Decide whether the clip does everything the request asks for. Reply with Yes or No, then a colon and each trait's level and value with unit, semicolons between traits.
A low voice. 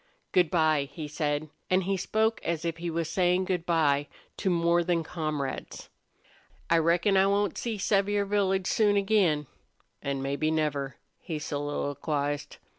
No: medium, 170 Hz